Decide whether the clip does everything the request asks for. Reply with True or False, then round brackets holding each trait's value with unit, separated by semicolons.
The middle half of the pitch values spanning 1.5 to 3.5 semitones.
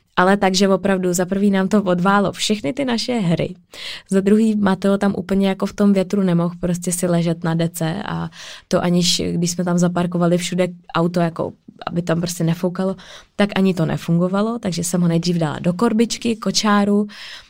True (2.5 semitones)